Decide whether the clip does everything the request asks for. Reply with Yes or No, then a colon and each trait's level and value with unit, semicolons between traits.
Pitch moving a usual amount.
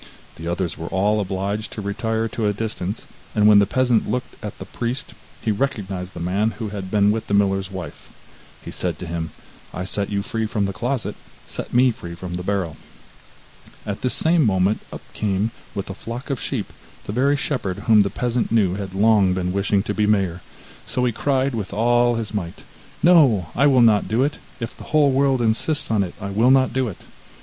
Yes: average, 3.8 semitones